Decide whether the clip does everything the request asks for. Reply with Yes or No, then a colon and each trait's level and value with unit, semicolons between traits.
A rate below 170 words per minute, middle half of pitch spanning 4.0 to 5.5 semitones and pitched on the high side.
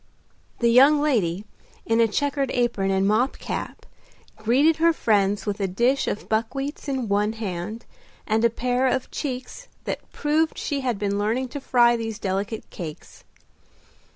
Yes: average, 155 wpm; average, 4.4 semitones; high, 235 Hz